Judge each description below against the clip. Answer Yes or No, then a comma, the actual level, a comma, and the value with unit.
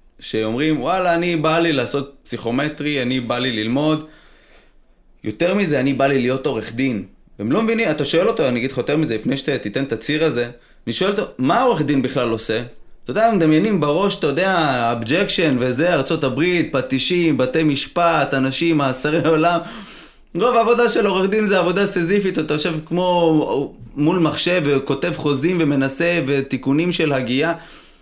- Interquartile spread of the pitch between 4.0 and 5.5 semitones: Yes, average, 4.3 semitones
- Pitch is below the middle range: No, medium, 155 Hz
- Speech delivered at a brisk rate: Yes, fast, 165 wpm